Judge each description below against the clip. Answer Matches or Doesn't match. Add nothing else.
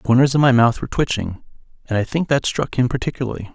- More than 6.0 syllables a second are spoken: Matches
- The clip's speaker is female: Doesn't match